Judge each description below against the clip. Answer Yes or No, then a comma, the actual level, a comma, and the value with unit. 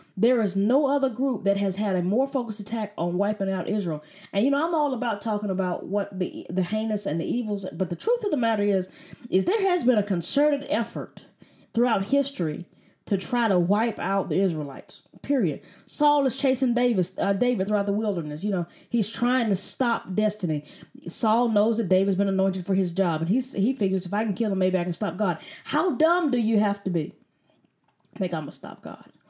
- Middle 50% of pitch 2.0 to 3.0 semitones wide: No, average, 4.5 semitones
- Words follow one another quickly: Yes, fast, 220 wpm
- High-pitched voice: Yes, high, 205 Hz